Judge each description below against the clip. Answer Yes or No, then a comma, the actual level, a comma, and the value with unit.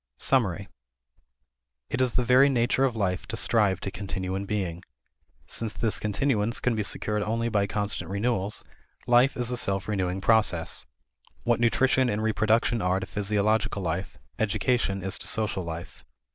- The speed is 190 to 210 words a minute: No, average, 160 wpm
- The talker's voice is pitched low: Yes, low, 105 Hz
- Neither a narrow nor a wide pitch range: Yes, average, 3.2 semitones